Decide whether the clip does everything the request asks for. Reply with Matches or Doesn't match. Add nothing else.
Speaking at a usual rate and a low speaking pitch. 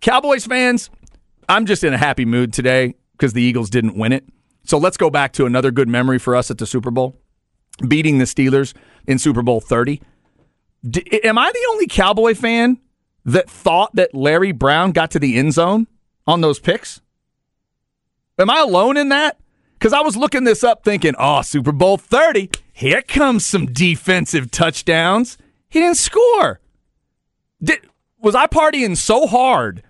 Doesn't match